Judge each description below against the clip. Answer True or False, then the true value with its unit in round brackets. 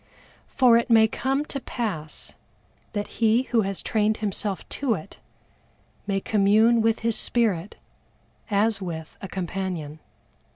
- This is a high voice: True (215 Hz)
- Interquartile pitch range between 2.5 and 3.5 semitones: True (3.1 semitones)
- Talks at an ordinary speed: False (130 wpm)